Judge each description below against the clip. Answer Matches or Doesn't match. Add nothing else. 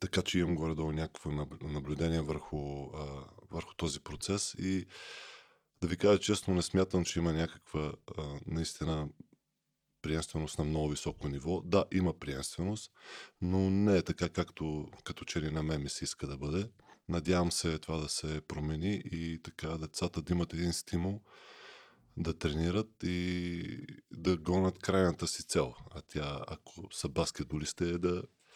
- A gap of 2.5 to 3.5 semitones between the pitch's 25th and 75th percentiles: Matches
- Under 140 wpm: Doesn't match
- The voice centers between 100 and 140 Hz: Doesn't match